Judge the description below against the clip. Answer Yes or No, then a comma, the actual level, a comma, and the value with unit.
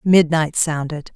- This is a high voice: No, medium, 160 Hz